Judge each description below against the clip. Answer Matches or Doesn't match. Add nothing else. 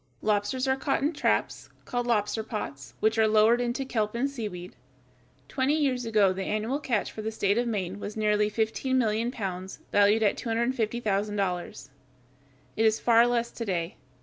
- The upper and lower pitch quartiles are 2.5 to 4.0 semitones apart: Matches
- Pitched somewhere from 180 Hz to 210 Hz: Doesn't match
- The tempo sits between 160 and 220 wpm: Matches